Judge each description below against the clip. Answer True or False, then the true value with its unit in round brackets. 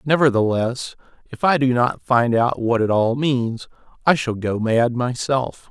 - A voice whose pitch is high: False (125 Hz)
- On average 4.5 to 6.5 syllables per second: False (4.0 syllables/s)